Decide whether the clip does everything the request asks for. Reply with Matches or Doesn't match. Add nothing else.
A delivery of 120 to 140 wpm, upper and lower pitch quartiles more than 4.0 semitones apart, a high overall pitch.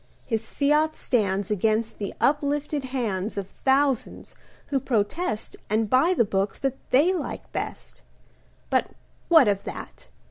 Matches